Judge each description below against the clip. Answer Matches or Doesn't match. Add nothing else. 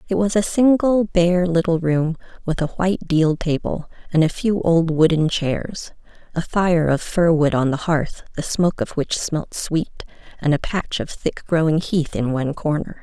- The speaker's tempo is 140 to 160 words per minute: Doesn't match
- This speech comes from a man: Doesn't match